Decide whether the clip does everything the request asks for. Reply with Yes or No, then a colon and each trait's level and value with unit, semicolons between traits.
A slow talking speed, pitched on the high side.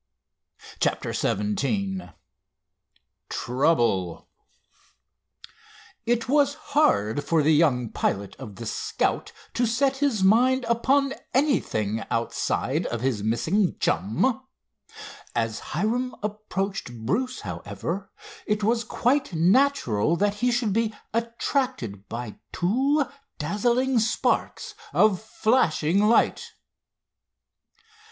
Yes: slow, 95 wpm; high, 205 Hz